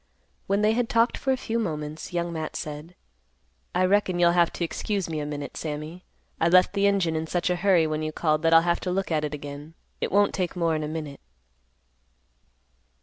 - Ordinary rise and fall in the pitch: Yes, average, 3.3 semitones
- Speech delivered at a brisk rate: Yes, fast, 210 wpm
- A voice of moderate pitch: Yes, medium, 170 Hz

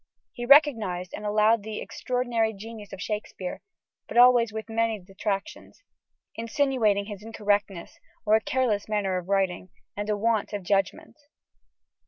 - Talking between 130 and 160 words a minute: Yes, average, 140 wpm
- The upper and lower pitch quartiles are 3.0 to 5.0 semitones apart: No, narrow, 2.4 semitones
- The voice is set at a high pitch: Yes, high, 215 Hz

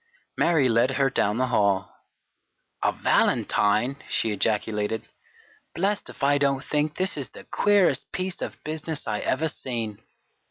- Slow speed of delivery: No, average, 145 wpm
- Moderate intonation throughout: No, wide, 6.1 semitones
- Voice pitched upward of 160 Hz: No, low, 135 Hz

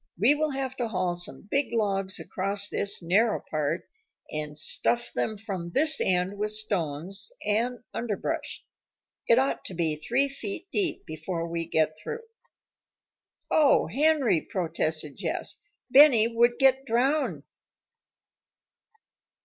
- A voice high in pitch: Yes, high, 210 Hz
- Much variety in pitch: Yes, wide, 7.2 semitones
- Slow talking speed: Yes, slow, 125 wpm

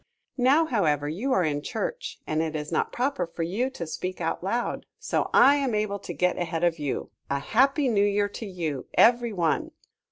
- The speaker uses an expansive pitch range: Yes, wide, 7.0 semitones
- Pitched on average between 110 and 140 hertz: No, high, 195 Hz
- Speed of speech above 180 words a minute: Yes, average, 200 wpm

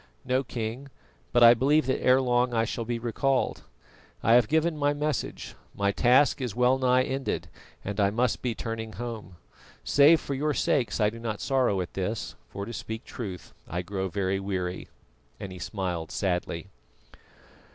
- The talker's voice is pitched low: Yes, low, 115 Hz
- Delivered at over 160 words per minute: Yes, average, 170 wpm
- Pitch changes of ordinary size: Yes, average, 4.6 semitones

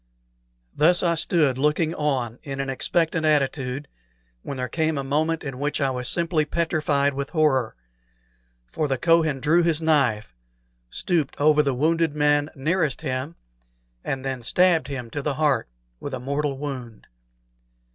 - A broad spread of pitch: No, average, 2.9 semitones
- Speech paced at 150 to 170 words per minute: Yes, average, 155 wpm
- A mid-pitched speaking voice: Yes, medium, 145 Hz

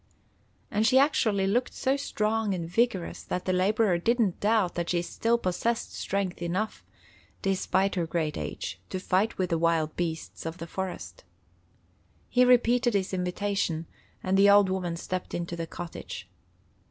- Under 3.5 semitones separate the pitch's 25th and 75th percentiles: No, average, 4.1 semitones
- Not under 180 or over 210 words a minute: No, average, 155 wpm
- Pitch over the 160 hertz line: Yes, high, 190 Hz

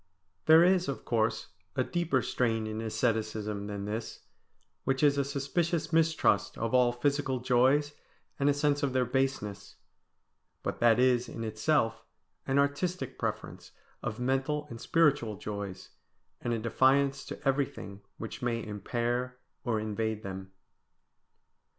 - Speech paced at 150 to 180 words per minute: No, average, 140 wpm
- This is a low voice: Yes, low, 125 Hz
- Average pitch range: Yes, average, 4.3 semitones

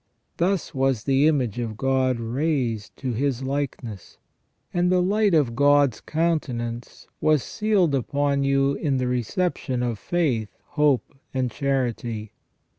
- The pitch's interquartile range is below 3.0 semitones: No, average, 3.9 semitones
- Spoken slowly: Yes, slow, 130 wpm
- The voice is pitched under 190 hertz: Yes, low, 135 Hz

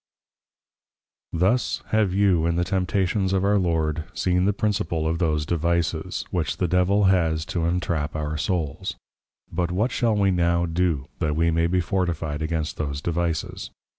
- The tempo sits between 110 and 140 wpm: No, average, 165 wpm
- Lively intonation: No, average, 2.8 semitones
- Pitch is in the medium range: No, very low, 85 Hz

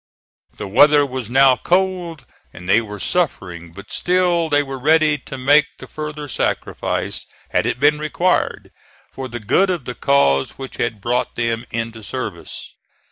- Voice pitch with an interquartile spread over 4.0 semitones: Yes, average, 5.1 semitones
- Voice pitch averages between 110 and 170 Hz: Yes, low, 135 Hz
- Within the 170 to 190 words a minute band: No, average, 160 wpm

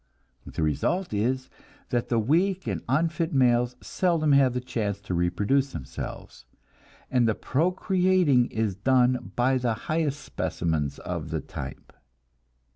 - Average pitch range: No, wide, 6.2 semitones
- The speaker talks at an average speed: No, slow, 130 wpm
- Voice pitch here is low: Yes, low, 125 Hz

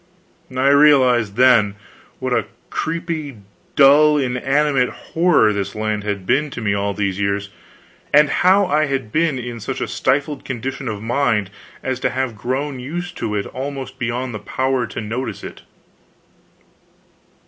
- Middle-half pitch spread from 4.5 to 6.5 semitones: Yes, average, 4.9 semitones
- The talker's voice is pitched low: Yes, low, 130 Hz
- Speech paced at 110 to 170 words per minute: Yes, average, 150 wpm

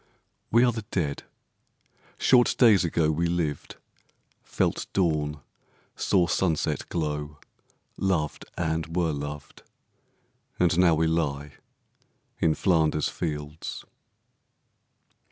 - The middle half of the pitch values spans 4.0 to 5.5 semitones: No, average, 2.8 semitones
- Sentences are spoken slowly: Yes, slow, 100 wpm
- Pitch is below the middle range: Yes, very low, 80 Hz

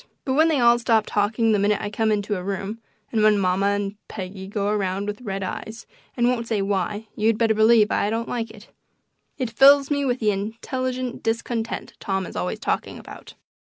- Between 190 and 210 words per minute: Yes, average, 200 wpm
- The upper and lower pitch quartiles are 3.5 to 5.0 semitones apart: No, narrow, 2.6 semitones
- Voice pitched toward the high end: Yes, high, 215 Hz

